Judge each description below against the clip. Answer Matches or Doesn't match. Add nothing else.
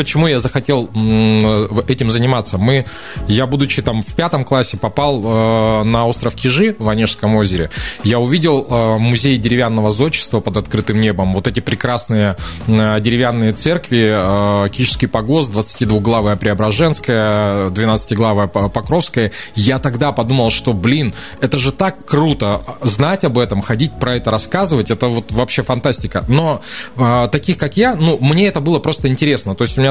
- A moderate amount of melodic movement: Matches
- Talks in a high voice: Doesn't match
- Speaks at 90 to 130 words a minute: Doesn't match